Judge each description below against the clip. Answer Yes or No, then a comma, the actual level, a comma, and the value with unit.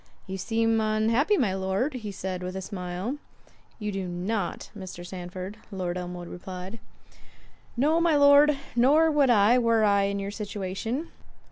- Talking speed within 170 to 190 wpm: No, average, 145 wpm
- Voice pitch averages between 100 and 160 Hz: No, high, 205 Hz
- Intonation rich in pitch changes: No, average, 4.6 semitones